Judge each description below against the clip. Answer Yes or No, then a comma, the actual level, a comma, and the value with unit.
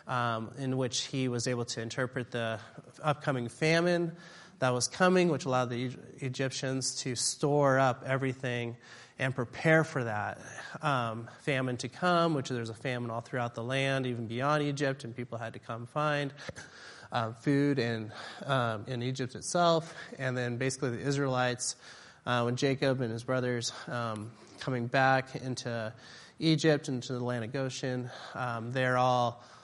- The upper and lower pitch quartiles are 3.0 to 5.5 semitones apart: No, narrow, 2.6 semitones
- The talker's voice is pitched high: No, low, 130 Hz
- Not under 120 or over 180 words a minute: Yes, average, 160 wpm